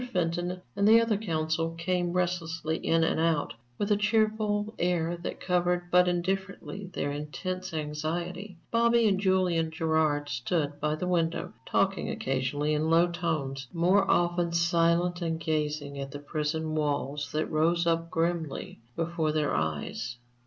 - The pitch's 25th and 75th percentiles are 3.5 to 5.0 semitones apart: No, average, 2.7 semitones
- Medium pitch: Yes, medium, 165 Hz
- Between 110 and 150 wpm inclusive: Yes, average, 145 wpm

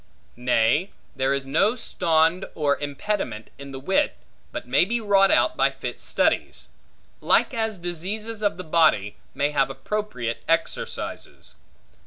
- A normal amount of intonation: No, wide, 7.1 semitones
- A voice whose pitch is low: No, medium, 165 Hz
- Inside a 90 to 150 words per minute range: Yes, average, 140 wpm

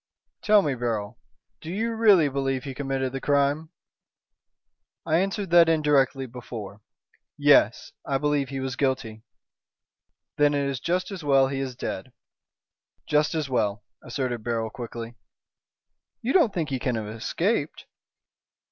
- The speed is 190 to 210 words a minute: No, average, 140 wpm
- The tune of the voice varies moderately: Yes, average, 4.2 semitones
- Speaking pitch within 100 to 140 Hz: Yes, low, 135 Hz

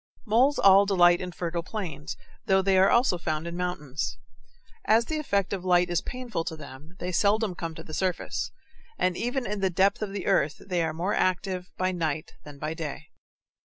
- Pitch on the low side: No, medium, 180 Hz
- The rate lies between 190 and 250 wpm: Yes, average, 195 wpm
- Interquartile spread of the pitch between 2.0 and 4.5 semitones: Yes, average, 3.2 semitones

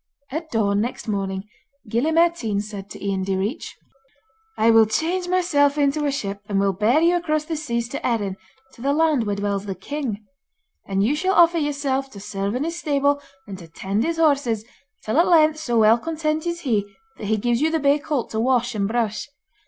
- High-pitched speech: Yes, high, 245 Hz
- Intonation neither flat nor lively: No, wide, 6.9 semitones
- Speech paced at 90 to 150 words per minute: No, fast, 205 wpm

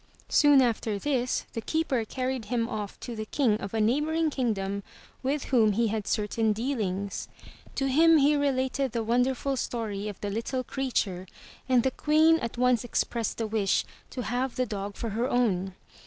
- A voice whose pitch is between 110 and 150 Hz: No, high, 240 Hz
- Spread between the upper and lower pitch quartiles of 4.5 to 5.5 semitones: No, average, 3.8 semitones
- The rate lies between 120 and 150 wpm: No, average, 175 wpm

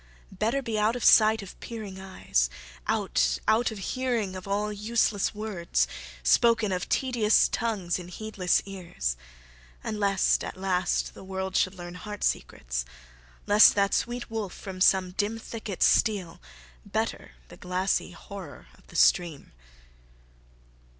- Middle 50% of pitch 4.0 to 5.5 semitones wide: No, average, 3.1 semitones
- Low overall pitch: No, high, 200 Hz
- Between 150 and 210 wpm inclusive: No, average, 140 wpm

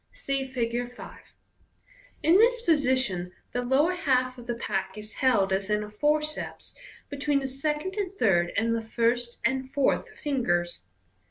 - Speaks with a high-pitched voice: Yes, very high, 255 Hz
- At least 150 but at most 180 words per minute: Yes, average, 155 wpm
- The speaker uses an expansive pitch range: No, average, 4.7 semitones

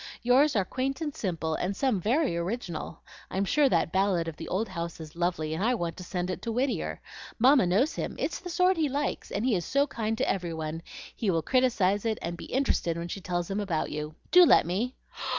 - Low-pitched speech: No, high, 195 Hz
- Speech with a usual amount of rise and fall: No, wide, 7.0 semitones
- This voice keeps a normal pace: No, fast, 230 wpm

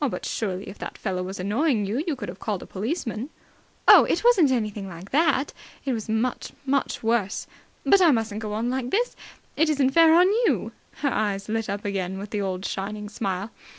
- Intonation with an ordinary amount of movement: No, wide, 5.7 semitones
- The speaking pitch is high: Yes, high, 220 Hz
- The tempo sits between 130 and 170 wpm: No, fast, 205 wpm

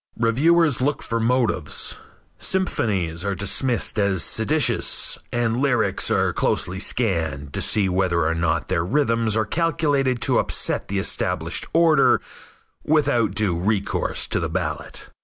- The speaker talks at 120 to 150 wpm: Yes, slow, 135 wpm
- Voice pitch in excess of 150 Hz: No, low, 110 Hz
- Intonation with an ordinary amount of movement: No, wide, 6.4 semitones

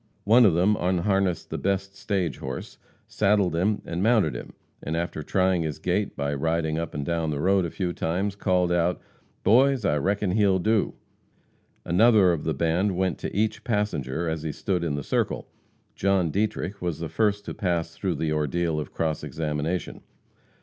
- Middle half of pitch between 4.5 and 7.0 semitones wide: No, average, 3.6 semitones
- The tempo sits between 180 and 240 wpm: Yes, average, 185 wpm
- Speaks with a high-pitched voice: No, very low, 90 Hz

